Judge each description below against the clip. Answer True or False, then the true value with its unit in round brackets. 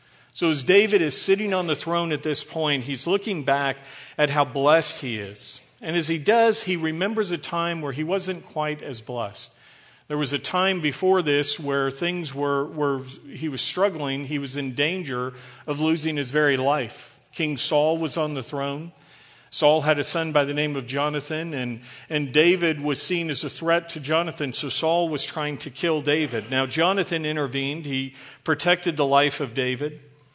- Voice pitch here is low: False (150 Hz)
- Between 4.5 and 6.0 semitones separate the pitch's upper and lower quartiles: False (2.9 semitones)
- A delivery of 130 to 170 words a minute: False (190 wpm)